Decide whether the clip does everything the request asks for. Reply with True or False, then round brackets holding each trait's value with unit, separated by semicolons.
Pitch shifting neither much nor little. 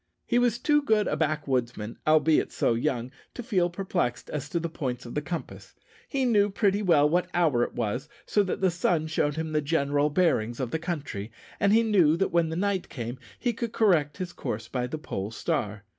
False (6.5 semitones)